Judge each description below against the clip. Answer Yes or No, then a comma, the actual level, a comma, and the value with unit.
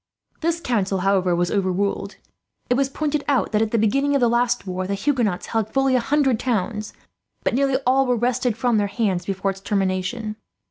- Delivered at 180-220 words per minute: Yes, average, 195 wpm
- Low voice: No, high, 225 Hz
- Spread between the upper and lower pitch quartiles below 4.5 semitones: No, average, 4.8 semitones